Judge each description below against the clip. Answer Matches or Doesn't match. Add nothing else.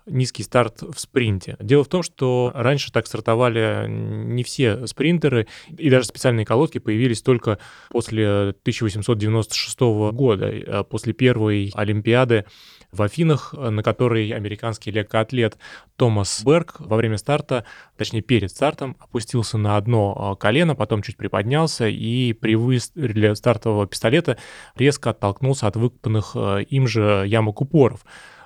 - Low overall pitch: Matches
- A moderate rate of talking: Matches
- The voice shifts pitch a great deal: Doesn't match